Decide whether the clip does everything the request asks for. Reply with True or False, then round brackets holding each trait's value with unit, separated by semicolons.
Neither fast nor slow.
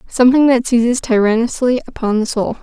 True (160 wpm)